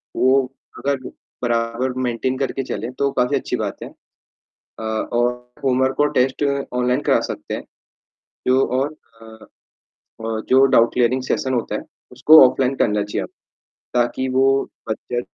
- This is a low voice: Yes, low, 125 Hz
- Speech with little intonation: Yes, narrow, 1.9 semitones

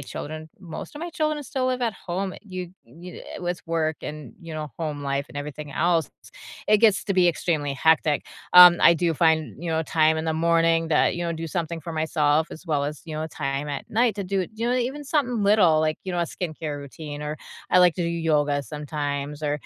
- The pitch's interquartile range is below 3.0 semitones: No, average, 3.3 semitones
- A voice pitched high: No, medium, 160 Hz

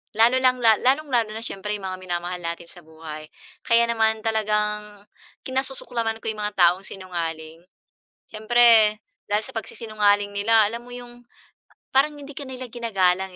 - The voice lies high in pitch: Yes, high, 215 Hz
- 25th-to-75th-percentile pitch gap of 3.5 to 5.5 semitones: Yes, average, 3.9 semitones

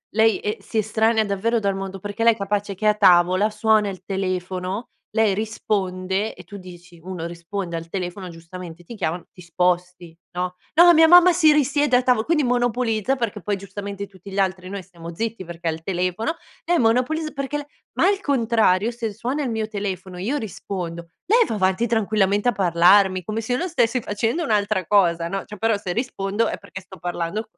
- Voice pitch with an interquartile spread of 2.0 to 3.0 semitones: No, average, 3.8 semitones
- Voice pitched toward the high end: Yes, high, 200 Hz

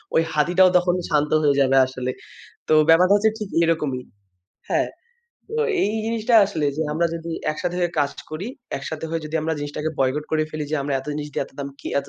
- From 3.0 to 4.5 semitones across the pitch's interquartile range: Yes, average, 3.3 semitones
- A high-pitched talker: No, medium, 155 Hz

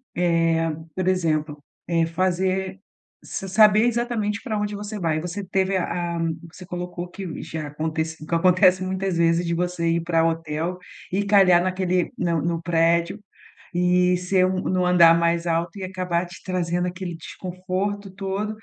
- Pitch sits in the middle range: Yes, medium, 180 Hz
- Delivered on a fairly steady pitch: Yes, narrow, 2.0 semitones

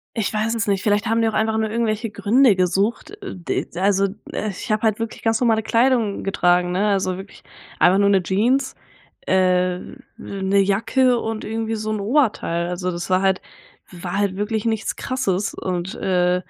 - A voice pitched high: Yes, high, 205 Hz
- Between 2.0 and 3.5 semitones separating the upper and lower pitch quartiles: Yes, average, 3.1 semitones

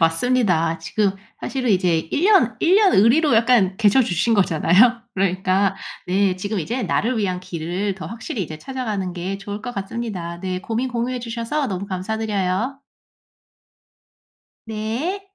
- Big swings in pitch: No, average, 4.6 semitones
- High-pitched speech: Yes, high, 205 Hz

